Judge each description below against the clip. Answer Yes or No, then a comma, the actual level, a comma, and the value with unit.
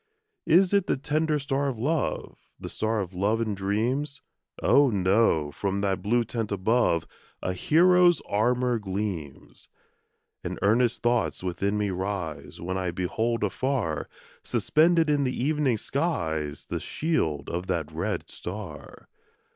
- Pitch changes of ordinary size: No, wide, 6.8 semitones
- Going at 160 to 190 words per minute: No, average, 140 wpm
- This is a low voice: Yes, low, 110 Hz